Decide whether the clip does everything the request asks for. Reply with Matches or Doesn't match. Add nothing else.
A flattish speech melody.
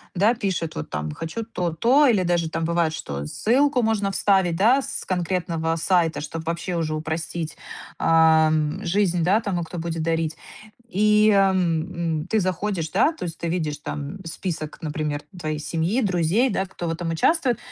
Doesn't match